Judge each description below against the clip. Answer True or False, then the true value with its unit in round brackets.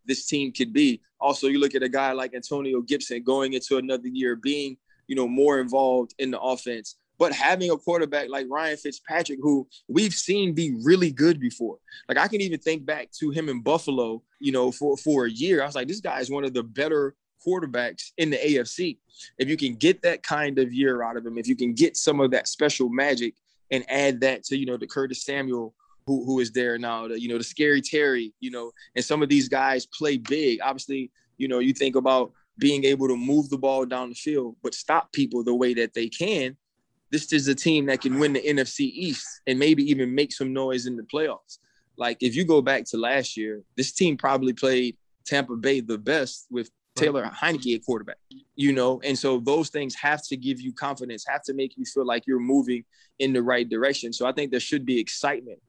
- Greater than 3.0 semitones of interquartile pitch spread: False (2.7 semitones)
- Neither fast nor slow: False (225 wpm)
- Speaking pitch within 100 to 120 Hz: False (135 Hz)